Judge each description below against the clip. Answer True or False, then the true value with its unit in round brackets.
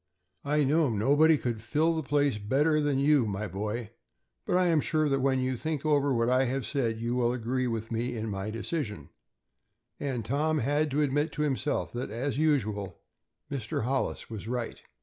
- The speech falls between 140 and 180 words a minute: False (190 wpm)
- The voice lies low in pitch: True (130 Hz)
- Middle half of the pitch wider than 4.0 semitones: True (4.4 semitones)